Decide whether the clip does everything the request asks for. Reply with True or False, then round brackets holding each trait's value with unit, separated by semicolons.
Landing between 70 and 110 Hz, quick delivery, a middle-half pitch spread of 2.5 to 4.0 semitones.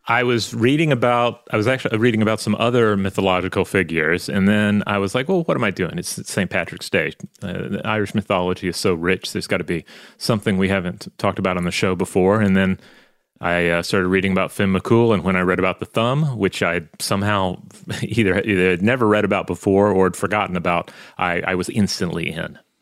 True (100 Hz; 215 wpm; 2.8 semitones)